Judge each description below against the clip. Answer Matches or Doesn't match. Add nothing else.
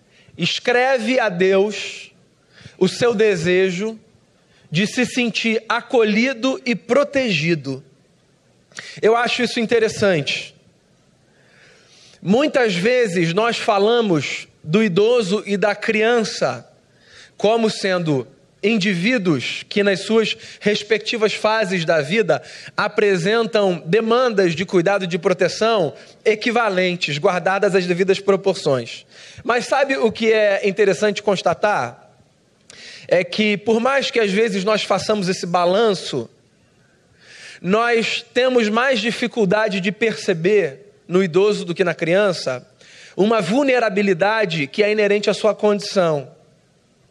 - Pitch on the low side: Doesn't match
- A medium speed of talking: Doesn't match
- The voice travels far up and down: Doesn't match